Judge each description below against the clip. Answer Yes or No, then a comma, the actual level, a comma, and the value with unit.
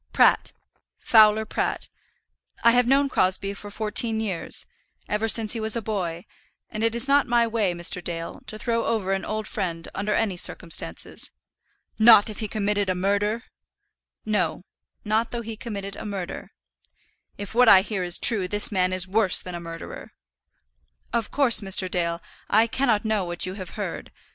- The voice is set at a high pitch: Yes, high, 210 Hz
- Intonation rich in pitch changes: No, average, 3.3 semitones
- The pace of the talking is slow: No, average, 175 wpm